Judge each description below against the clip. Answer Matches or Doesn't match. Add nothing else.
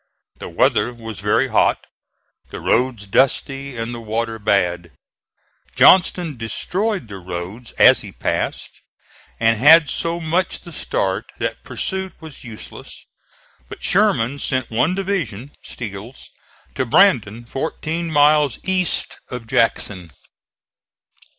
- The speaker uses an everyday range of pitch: Doesn't match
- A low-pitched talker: Matches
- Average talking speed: Doesn't match